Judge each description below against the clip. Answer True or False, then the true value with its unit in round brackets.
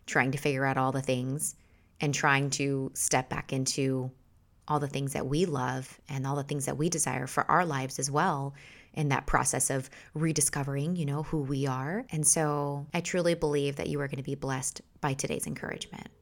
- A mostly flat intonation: True (2.3 semitones)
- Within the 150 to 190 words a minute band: False (205 wpm)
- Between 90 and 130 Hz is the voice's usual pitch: False (140 Hz)